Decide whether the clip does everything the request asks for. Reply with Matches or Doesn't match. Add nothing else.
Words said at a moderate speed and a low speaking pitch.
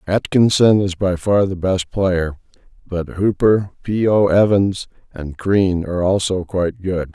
Matches